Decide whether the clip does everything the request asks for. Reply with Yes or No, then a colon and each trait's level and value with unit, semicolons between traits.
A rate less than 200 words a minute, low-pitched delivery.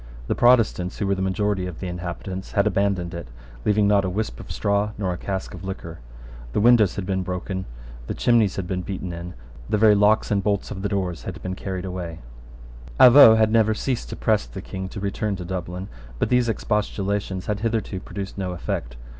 No: fast, 205 wpm; low, 100 Hz